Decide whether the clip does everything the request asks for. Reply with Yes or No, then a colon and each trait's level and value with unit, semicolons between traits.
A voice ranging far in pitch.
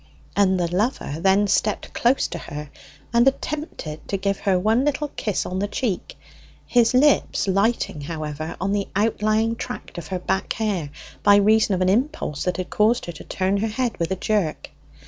No: average, 3.7 semitones